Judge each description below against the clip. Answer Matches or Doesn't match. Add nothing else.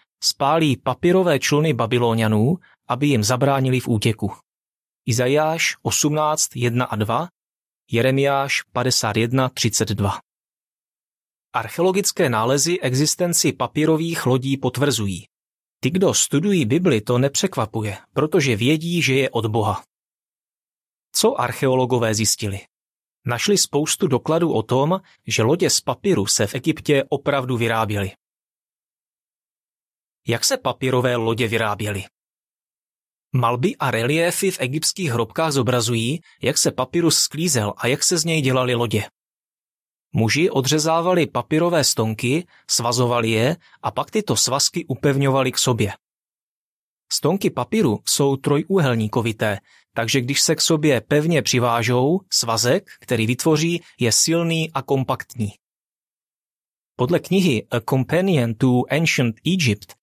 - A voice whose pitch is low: Matches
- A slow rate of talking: Matches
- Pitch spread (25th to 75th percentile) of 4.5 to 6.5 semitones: Matches